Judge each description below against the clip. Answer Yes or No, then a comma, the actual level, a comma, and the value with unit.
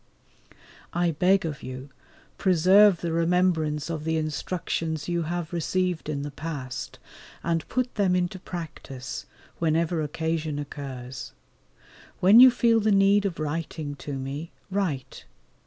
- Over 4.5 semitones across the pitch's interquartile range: No, average, 3.4 semitones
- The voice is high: No, medium, 165 Hz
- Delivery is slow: Yes, slow, 130 wpm